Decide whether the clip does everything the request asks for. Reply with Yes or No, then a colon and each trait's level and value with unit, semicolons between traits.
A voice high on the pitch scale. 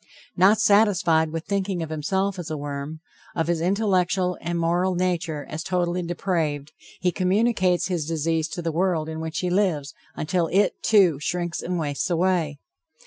No: medium, 175 Hz